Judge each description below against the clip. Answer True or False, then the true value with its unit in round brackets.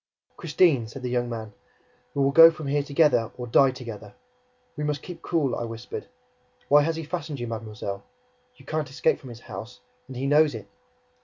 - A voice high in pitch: False (135 Hz)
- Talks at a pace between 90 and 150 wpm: False (190 wpm)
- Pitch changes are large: False (4.5 semitones)